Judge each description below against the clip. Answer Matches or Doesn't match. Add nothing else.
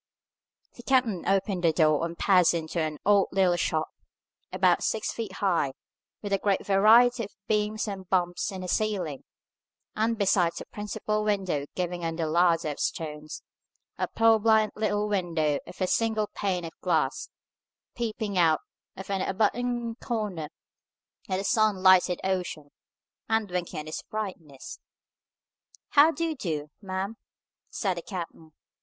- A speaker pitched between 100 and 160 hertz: Doesn't match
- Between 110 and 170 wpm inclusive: Matches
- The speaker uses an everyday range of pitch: Matches